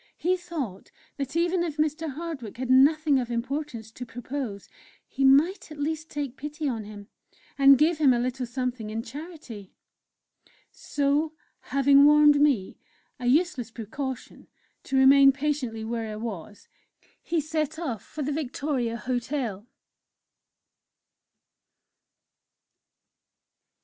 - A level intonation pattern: No, average, 4.1 semitones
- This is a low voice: No, very high, 275 Hz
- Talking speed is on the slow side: Yes, slow, 125 wpm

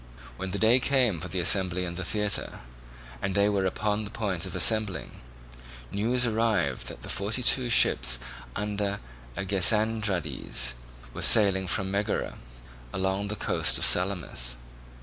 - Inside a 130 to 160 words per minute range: Yes, average, 145 wpm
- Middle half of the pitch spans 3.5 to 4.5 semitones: No, narrow, 2.6 semitones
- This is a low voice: Yes, low, 100 Hz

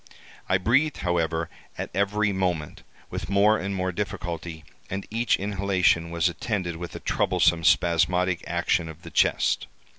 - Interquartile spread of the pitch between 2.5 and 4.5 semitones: Yes, average, 2.9 semitones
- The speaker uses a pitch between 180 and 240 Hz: No, very low, 90 Hz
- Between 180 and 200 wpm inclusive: No, average, 145 wpm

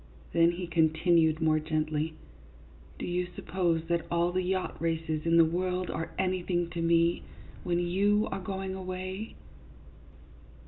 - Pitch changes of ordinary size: No, narrow, 2.2 semitones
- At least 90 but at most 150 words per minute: Yes, average, 145 wpm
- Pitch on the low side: No, medium, 170 Hz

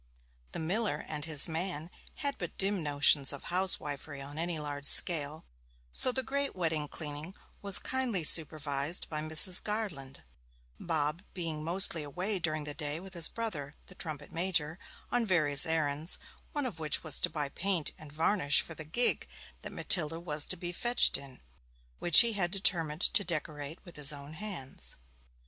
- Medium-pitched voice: Yes, medium, 160 Hz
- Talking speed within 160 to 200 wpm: Yes, average, 165 wpm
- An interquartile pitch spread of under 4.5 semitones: Yes, average, 4.0 semitones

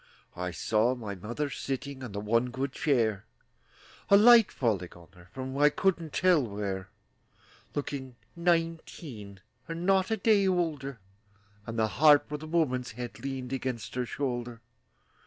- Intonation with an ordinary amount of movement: No, wide, 6.1 semitones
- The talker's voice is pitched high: No, low, 130 Hz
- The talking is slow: No, average, 150 wpm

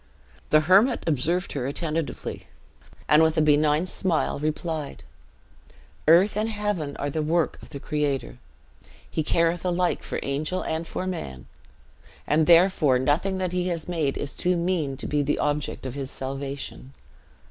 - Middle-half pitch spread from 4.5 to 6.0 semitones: No, average, 3.6 semitones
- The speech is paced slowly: No, average, 155 wpm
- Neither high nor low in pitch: Yes, medium, 155 Hz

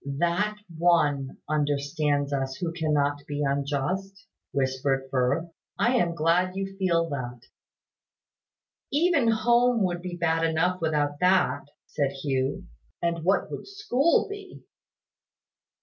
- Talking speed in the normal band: No, slow, 120 wpm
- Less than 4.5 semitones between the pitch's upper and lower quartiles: No, average, 5.1 semitones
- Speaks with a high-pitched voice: No, medium, 165 Hz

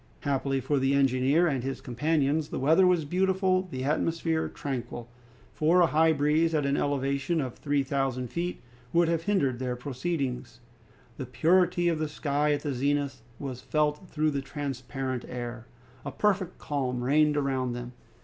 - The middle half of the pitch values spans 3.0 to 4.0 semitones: Yes, average, 3.6 semitones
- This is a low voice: No, medium, 145 Hz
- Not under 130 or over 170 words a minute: Yes, average, 165 wpm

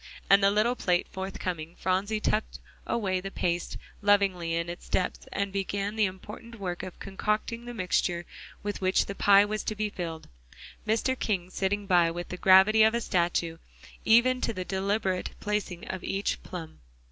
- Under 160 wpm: No, average, 170 wpm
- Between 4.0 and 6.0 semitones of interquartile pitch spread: No, average, 2.8 semitones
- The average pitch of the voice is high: Yes, high, 195 Hz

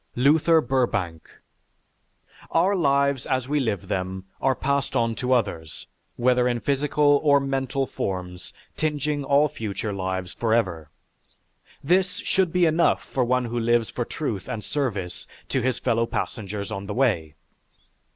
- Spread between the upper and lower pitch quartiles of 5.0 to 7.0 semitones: Yes, wide, 5.6 semitones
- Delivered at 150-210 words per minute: No, average, 140 wpm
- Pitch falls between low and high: No, low, 125 Hz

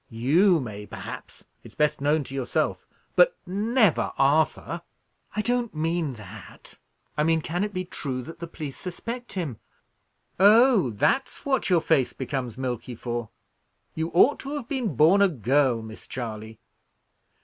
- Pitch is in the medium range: Yes, medium, 155 Hz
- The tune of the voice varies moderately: No, wide, 7.7 semitones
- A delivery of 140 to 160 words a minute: Yes, average, 150 wpm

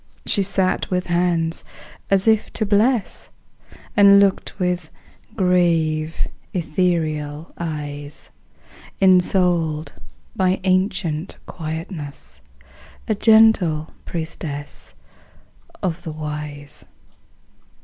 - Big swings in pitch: No, average, 3.5 semitones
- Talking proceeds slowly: Yes, slow, 80 wpm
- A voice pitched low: No, medium, 170 Hz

